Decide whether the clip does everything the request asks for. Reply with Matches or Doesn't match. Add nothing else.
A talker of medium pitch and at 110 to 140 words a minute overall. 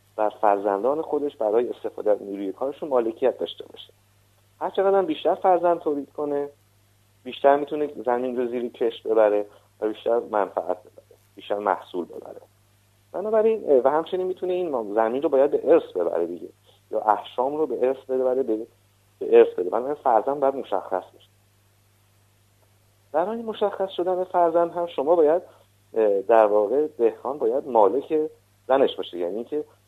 Doesn't match